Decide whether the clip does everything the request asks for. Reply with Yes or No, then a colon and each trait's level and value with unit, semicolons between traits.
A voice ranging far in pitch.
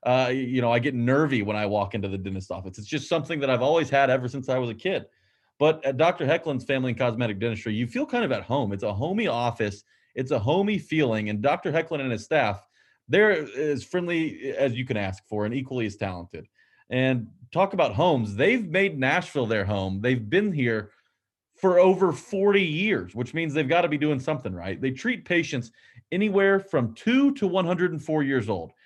Yes: wide, 6.4 semitones